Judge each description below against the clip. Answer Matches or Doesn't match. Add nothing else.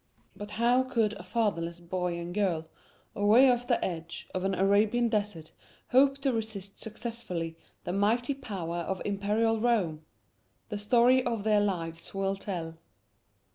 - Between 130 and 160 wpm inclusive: Matches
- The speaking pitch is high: Matches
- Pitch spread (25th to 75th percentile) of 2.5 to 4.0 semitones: Doesn't match